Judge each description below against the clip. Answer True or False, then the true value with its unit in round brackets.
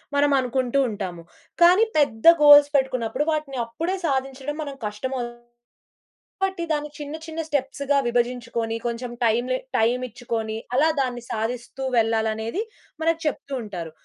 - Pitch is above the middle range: True (255 Hz)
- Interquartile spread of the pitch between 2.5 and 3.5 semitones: False (4.0 semitones)